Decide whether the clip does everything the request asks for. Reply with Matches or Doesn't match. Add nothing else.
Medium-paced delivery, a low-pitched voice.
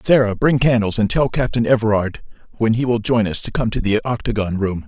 Doesn't match